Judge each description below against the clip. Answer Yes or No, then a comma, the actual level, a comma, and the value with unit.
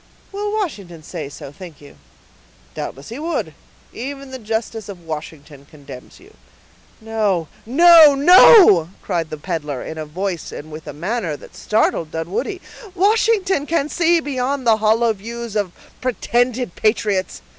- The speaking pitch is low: No, high, 220 Hz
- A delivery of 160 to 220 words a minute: No, average, 145 wpm